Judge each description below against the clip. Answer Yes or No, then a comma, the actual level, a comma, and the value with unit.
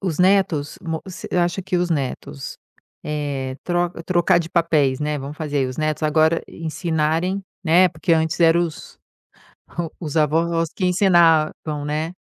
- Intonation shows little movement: Yes, narrow, 2.3 semitones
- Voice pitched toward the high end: No, medium, 160 Hz